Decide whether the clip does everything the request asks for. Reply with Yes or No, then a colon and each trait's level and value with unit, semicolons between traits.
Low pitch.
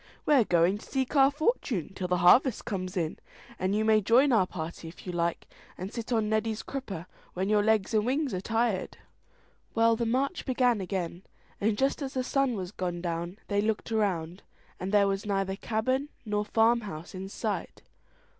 No: high, 210 Hz